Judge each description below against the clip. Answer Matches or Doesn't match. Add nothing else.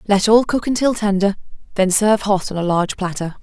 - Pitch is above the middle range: Matches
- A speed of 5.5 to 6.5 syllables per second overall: Matches